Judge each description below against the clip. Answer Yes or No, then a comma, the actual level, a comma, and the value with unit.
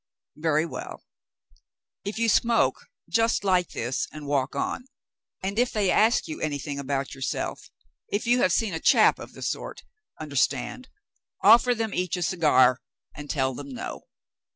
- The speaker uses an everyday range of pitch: No, wide, 7.7 semitones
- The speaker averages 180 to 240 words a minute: No, average, 155 wpm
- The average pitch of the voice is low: No, medium, 165 Hz